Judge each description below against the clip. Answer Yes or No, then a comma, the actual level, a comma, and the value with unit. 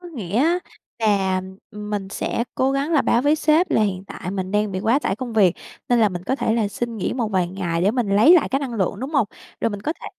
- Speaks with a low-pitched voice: No, high, 220 Hz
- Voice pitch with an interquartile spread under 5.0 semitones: No, average, 5.3 semitones